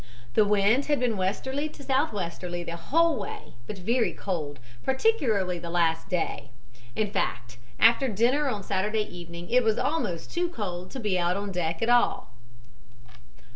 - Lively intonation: Yes, wide, 6.5 semitones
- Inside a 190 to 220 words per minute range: No, average, 160 wpm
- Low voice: No, high, 205 Hz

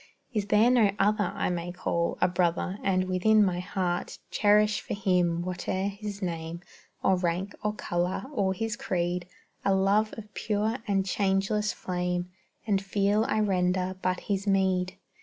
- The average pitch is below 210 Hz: Yes, high, 190 Hz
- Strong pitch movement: No, narrow, 2.5 semitones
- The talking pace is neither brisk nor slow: Yes, average, 160 wpm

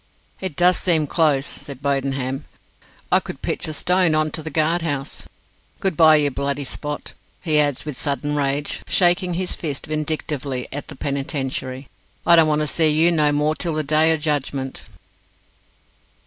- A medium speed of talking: Yes, average, 170 wpm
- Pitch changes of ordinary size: No, narrow, 2.3 semitones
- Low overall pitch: No, medium, 150 Hz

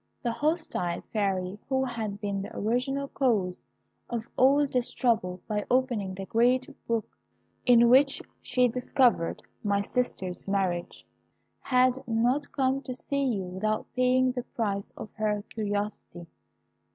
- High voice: Yes, high, 230 Hz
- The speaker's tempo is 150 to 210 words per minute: No, slow, 135 wpm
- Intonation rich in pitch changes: No, average, 4.2 semitones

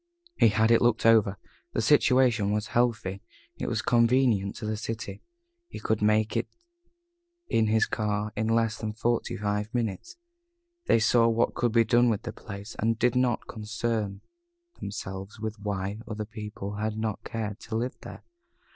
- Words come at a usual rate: Yes, average, 165 wpm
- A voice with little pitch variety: Yes, narrow, 1.7 semitones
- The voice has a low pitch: Yes, low, 110 Hz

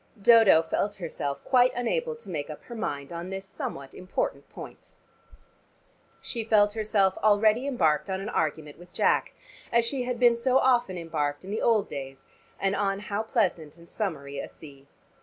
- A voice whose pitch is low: No, high, 195 Hz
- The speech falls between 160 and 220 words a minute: Yes, average, 175 wpm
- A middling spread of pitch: No, wide, 6.4 semitones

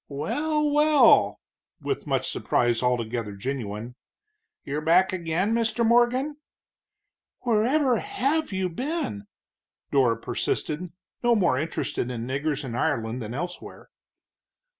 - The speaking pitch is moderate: Yes, medium, 170 Hz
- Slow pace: Yes, slow, 110 wpm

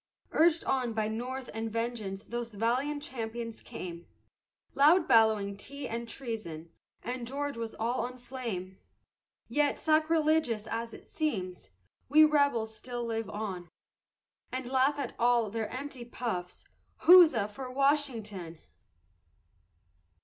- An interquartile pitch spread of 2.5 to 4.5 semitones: Yes, average, 4.0 semitones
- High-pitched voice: Yes, high, 235 Hz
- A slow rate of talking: Yes, slow, 120 wpm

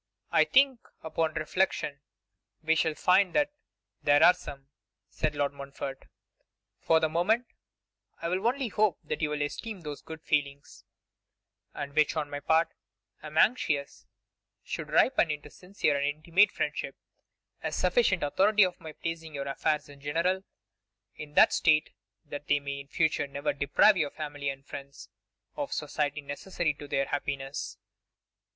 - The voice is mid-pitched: Yes, medium, 155 Hz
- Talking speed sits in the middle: Yes, average, 155 wpm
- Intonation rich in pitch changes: No, average, 3.8 semitones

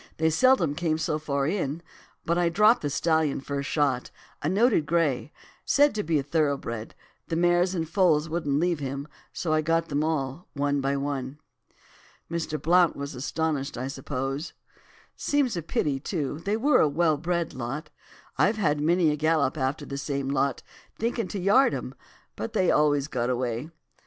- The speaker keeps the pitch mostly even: No, average, 3.6 semitones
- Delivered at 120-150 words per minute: No, average, 170 wpm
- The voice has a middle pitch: Yes, medium, 155 Hz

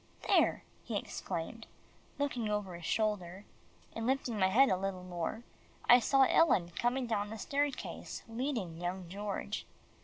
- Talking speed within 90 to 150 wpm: Yes, average, 145 wpm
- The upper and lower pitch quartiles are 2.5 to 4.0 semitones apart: No, average, 5.0 semitones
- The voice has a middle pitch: No, high, 210 Hz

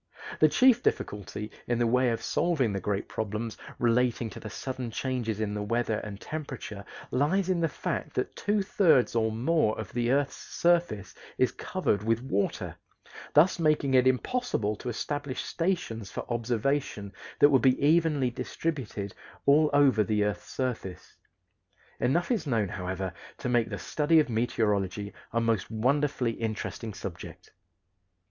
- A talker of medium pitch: No, low, 120 Hz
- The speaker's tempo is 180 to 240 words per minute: No, average, 155 wpm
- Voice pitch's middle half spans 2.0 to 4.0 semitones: No, average, 5.2 semitones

